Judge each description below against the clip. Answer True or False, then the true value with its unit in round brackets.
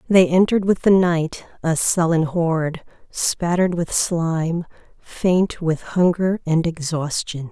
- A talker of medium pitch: True (170 Hz)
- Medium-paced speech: False (130 wpm)